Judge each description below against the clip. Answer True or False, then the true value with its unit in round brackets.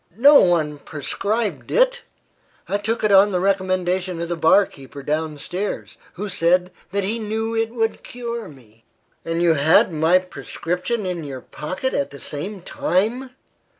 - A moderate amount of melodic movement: True (5.0 semitones)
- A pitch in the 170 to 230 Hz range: True (185 Hz)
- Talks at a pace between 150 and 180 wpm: True (160 wpm)